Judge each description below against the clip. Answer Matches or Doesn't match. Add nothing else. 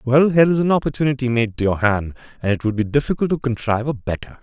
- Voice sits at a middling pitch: Doesn't match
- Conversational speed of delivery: Doesn't match